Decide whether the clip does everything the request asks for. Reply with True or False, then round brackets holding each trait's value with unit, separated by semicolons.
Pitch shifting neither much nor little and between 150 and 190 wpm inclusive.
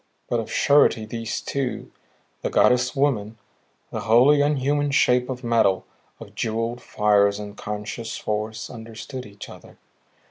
False (3.3 semitones; 140 wpm)